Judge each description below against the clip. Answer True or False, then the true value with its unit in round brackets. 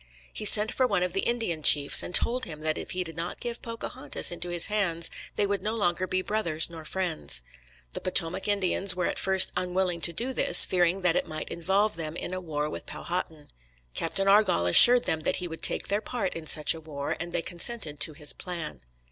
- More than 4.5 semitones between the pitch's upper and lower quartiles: False (3.6 semitones)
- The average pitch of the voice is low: False (180 Hz)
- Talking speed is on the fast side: True (220 wpm)